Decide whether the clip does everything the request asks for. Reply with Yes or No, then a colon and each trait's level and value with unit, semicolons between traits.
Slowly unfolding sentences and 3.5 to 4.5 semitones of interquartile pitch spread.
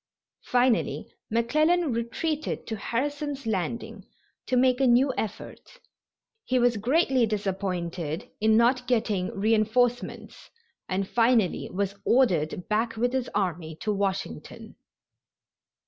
Yes: slow, 110 wpm; average, 4.2 semitones